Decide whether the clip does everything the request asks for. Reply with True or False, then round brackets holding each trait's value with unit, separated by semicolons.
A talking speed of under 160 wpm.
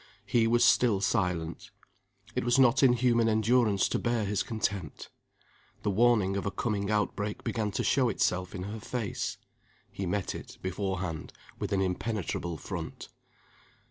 True (150 wpm)